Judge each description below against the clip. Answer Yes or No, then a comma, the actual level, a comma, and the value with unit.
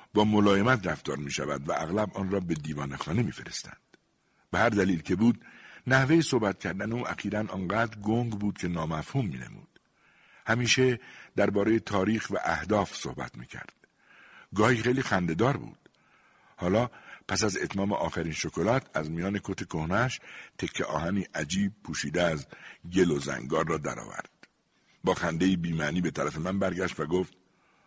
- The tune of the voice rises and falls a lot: No, average, 4.7 semitones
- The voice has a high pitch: No, very low, 95 Hz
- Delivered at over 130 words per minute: Yes, fast, 155 wpm